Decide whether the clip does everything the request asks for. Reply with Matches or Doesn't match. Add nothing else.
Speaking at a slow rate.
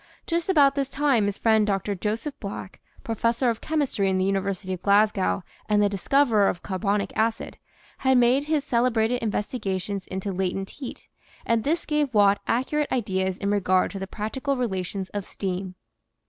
Doesn't match